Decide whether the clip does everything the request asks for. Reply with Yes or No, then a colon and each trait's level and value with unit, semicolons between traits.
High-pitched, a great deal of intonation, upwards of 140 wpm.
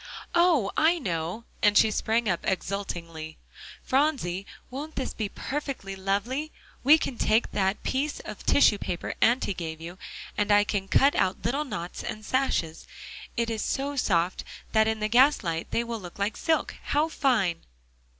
Yes: high, 215 Hz; wide, 6.2 semitones; average, 160 wpm